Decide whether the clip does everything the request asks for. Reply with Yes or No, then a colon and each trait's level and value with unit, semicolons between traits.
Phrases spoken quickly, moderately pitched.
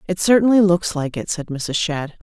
Yes: fast, 210 wpm; medium, 175 Hz